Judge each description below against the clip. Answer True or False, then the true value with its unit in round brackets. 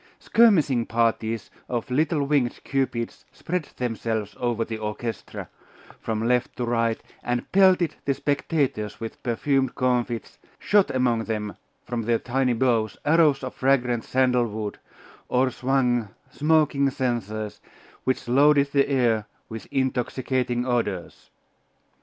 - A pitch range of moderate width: True (3.1 semitones)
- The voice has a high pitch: False (125 Hz)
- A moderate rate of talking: False (125 wpm)